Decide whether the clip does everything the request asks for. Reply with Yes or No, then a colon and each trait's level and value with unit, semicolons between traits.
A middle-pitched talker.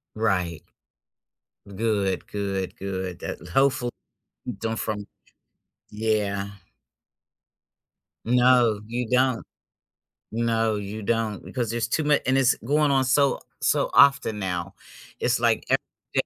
No: low, 110 Hz